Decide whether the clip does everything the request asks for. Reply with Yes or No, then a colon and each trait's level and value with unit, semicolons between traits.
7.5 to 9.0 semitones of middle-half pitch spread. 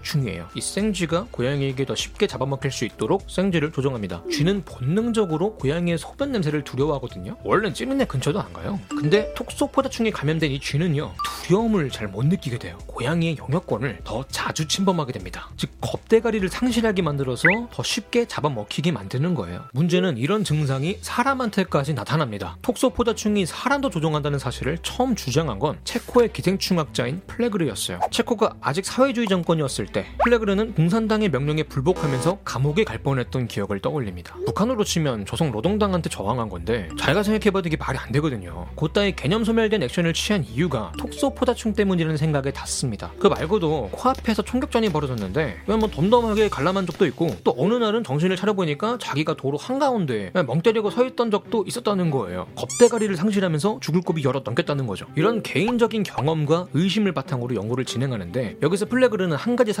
Yes: wide, 7.8 semitones